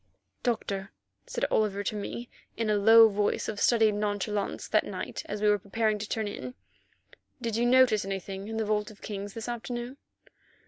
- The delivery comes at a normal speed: Yes, average, 175 wpm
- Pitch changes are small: Yes, narrow, 1.9 semitones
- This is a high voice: Yes, high, 215 Hz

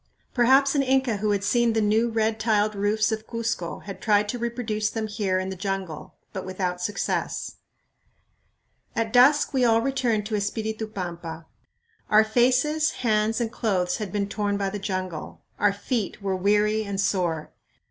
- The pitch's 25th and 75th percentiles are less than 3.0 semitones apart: Yes, narrow, 2.6 semitones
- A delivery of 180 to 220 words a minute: No, average, 170 wpm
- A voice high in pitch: Yes, high, 215 Hz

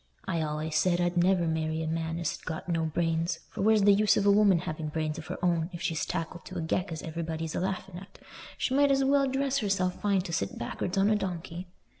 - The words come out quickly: Yes, fast, 245 wpm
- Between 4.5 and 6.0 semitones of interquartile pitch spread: No, average, 3.4 semitones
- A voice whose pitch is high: No, medium, 175 Hz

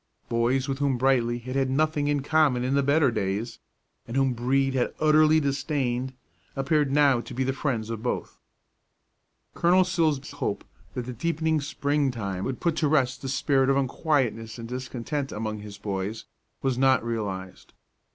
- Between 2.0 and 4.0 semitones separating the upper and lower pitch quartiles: Yes, average, 3.5 semitones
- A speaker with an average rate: Yes, average, 170 wpm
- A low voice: Yes, low, 130 Hz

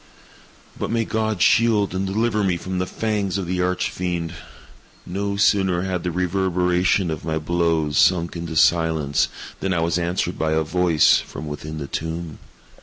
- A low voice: Yes, very low, 90 Hz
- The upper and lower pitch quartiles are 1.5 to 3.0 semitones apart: Yes, average, 2.7 semitones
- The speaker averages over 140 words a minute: Yes, average, 170 wpm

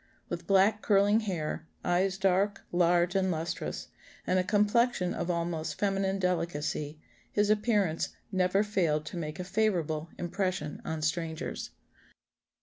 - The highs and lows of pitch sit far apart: No, average, 3.1 semitones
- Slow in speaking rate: Yes, slow, 130 wpm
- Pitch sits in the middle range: Yes, medium, 180 Hz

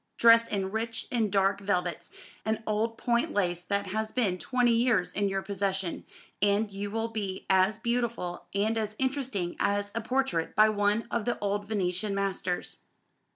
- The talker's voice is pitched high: Yes, high, 205 Hz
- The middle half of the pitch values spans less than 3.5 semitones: Yes, average, 2.8 semitones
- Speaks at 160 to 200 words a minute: Yes, average, 165 wpm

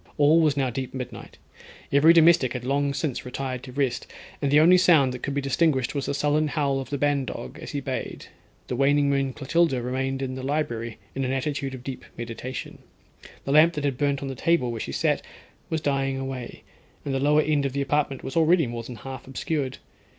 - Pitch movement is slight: Yes, narrow, 2.1 semitones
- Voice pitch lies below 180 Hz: Yes, low, 135 Hz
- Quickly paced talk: Yes, fast, 215 wpm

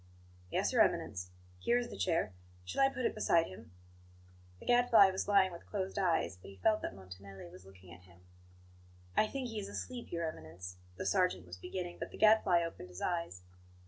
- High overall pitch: No, medium, 170 Hz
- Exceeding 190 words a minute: Yes, average, 200 wpm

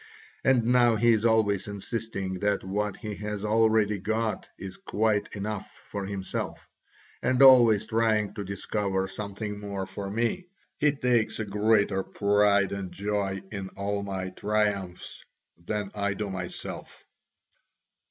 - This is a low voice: Yes, low, 105 Hz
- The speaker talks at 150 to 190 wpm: No, slow, 135 wpm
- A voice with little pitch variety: Yes, narrow, 2.0 semitones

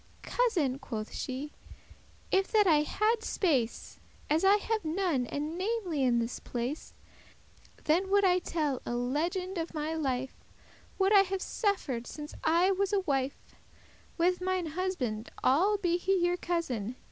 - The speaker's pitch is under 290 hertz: No, very high, 335 Hz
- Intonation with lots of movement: Yes, wide, 6.1 semitones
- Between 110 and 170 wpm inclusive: Yes, average, 155 wpm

